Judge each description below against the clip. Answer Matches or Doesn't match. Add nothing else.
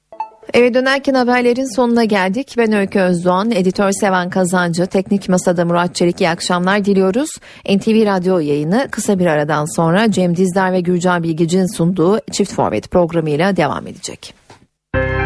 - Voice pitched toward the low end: Doesn't match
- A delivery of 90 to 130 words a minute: Doesn't match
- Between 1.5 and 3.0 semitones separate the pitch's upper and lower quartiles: Doesn't match